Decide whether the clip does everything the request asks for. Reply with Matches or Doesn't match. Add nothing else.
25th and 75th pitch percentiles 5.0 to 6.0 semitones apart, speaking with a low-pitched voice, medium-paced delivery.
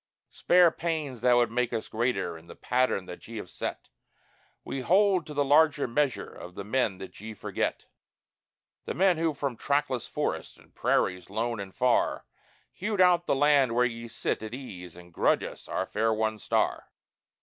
Matches